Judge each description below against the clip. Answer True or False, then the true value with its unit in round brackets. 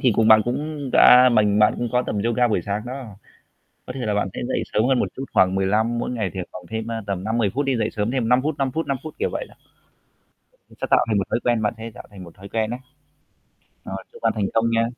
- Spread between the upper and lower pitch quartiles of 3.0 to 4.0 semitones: True (3.3 semitones)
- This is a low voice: True (115 Hz)